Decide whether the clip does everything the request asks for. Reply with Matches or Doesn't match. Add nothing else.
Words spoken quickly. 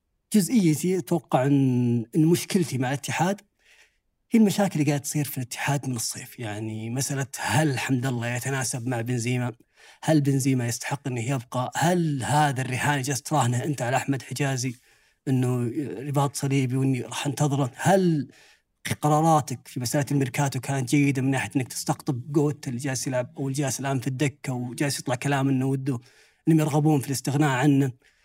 Matches